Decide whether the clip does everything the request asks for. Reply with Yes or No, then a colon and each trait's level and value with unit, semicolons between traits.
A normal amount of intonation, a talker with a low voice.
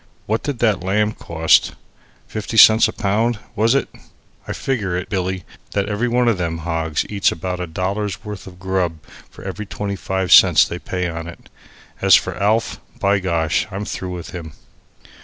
Yes: average, 3.2 semitones; very low, 95 Hz